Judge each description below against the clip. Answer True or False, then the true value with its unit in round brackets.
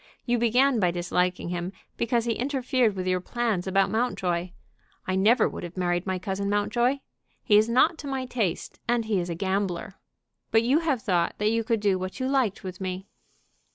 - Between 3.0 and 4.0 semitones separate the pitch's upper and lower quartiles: False (4.6 semitones)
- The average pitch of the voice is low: False (205 Hz)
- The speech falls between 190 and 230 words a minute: True (195 wpm)